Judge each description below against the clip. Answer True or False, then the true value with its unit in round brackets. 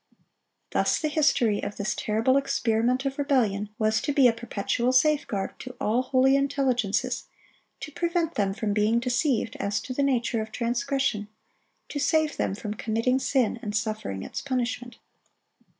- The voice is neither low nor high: False (245 Hz)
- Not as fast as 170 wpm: True (155 wpm)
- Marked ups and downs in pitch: False (4.1 semitones)